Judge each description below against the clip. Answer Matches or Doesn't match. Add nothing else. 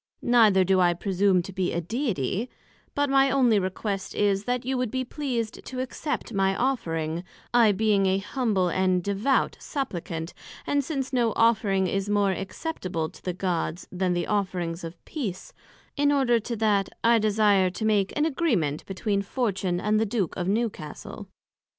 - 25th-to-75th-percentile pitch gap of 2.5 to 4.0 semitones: Doesn't match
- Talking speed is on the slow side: Doesn't match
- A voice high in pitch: Matches